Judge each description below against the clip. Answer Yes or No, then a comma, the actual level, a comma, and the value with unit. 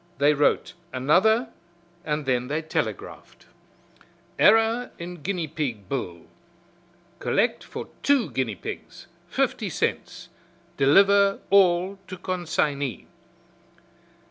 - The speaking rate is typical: No, slow, 95 wpm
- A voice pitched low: No, medium, 160 Hz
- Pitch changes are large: Yes, wide, 6.1 semitones